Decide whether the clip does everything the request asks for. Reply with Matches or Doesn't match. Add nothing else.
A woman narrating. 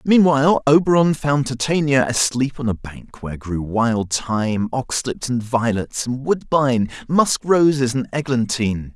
Doesn't match